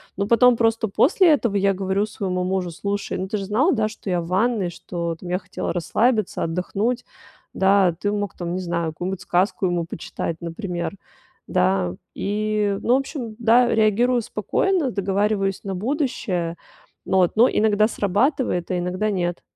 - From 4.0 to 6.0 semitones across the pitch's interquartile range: No, average, 3.6 semitones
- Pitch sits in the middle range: No, high, 200 Hz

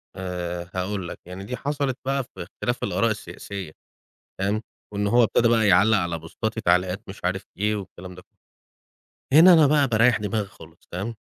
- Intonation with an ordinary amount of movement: Yes, average, 4.1 semitones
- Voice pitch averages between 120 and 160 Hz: No, low, 100 Hz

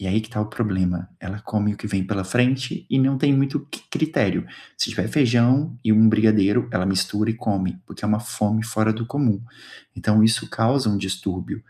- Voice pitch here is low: Yes, low, 110 Hz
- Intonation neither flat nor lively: Yes, average, 3.8 semitones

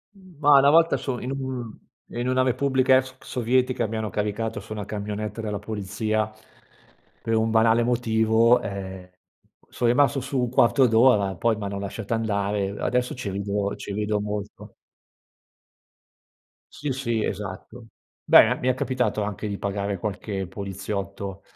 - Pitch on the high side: No, low, 110 Hz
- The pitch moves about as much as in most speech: Yes, average, 3.6 semitones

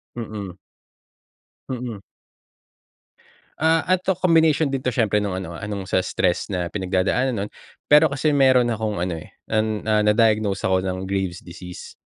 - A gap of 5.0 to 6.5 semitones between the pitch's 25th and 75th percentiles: Yes, wide, 5.6 semitones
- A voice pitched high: No, low, 105 Hz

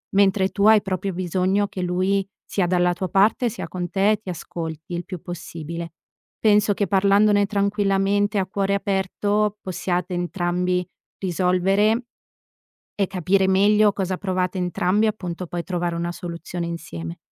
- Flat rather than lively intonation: Yes, narrow, 2.2 semitones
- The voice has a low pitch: No, high, 190 Hz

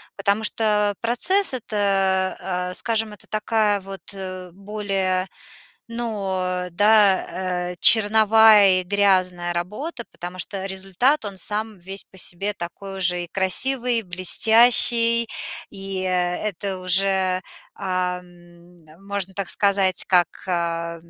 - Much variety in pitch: No, average, 2.7 semitones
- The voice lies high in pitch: Yes, high, 195 Hz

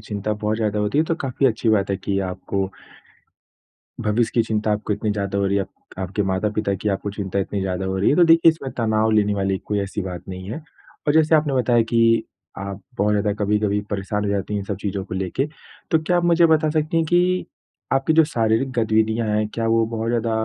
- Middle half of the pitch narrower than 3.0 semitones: No, average, 3.3 semitones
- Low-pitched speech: Yes, low, 105 Hz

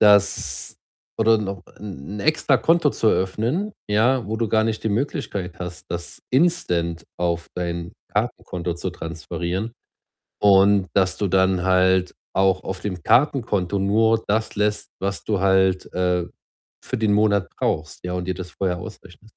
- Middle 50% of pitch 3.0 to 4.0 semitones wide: Yes, average, 3.3 semitones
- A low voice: Yes, very low, 95 Hz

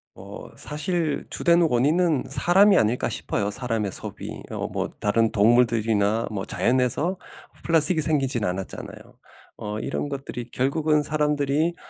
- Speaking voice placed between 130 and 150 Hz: Yes, low, 135 Hz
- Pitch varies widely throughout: Yes, wide, 5.7 semitones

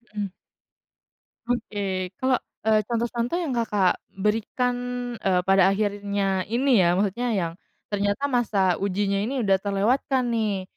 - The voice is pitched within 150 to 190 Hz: No, high, 205 Hz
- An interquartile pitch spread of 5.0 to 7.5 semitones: No, average, 3.6 semitones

